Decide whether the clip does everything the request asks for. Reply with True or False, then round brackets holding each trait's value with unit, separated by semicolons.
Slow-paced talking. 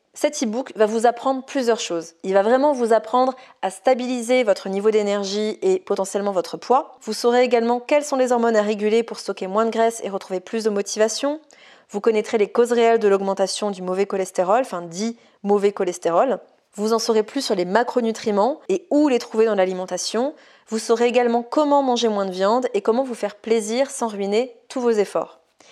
False (200 wpm)